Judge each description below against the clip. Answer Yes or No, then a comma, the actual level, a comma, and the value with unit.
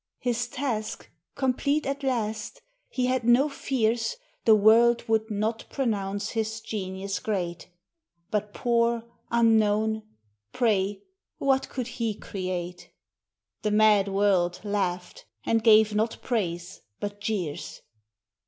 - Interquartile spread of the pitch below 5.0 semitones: Yes, average, 2.9 semitones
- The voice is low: No, high, 220 Hz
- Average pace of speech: No, slow, 115 wpm